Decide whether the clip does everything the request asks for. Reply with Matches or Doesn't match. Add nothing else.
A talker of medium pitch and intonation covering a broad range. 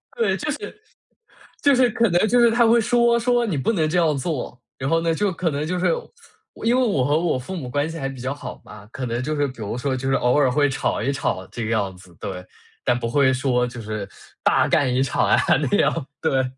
Matches